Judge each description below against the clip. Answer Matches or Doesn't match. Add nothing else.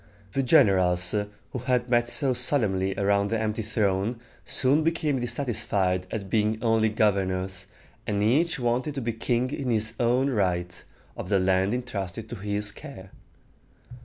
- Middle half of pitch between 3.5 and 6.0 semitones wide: Matches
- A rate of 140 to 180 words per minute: Matches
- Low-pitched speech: Matches